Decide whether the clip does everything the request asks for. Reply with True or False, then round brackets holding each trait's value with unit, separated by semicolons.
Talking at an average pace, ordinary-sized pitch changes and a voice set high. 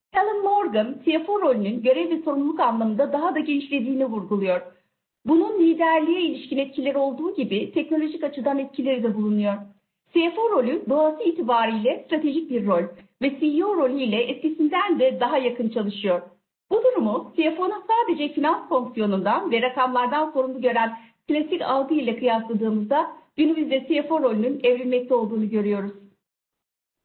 False (130 wpm; 5.7 semitones; 275 Hz)